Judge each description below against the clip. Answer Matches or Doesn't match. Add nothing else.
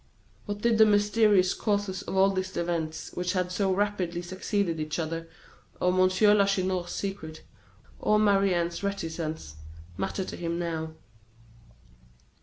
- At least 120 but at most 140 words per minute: Matches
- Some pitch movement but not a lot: Matches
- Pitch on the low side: Doesn't match